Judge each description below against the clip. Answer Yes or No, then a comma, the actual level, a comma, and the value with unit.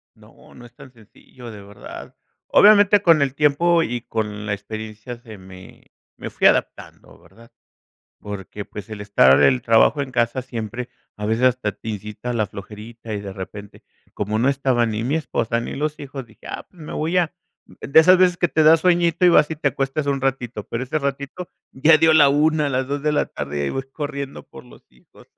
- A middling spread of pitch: No, wide, 5.7 semitones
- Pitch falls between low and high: No, low, 125 Hz